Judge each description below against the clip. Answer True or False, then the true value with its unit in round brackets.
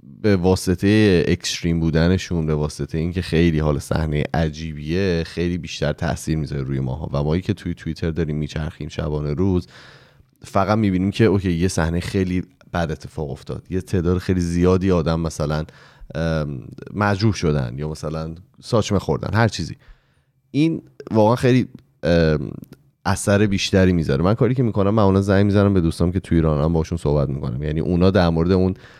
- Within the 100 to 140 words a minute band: False (155 wpm)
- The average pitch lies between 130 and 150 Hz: False (90 Hz)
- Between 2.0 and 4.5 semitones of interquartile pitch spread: True (3.8 semitones)